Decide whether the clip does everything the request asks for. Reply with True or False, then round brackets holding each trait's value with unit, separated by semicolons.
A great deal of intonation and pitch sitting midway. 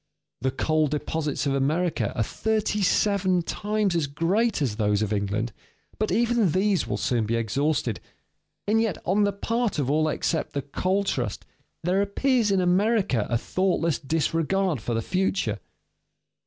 True (6.7 semitones; 170 Hz)